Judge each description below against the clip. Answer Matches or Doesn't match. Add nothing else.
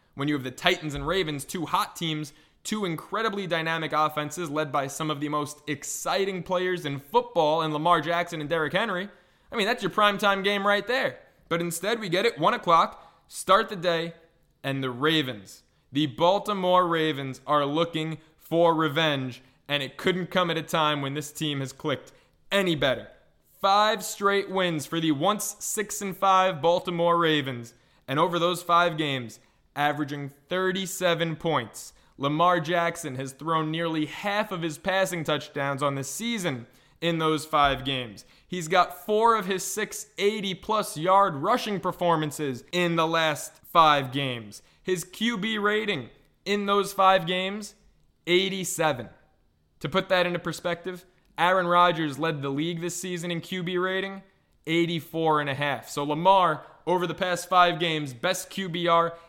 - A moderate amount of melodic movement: Matches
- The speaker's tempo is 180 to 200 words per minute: Doesn't match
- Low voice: Doesn't match